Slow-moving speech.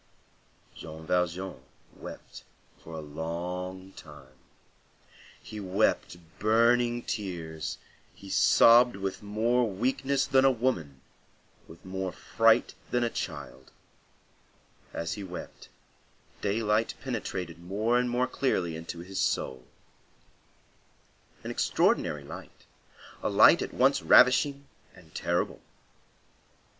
Yes: slow, 105 wpm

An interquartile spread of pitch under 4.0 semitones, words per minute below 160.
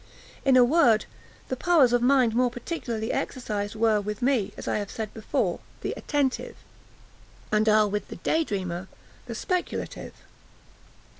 Yes: average, 3.6 semitones; average, 150 wpm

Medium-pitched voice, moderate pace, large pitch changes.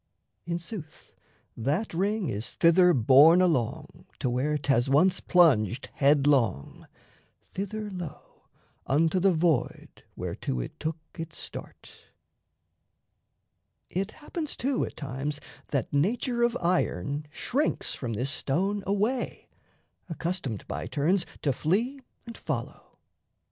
No: medium, 165 Hz; slow, 115 wpm; wide, 6.0 semitones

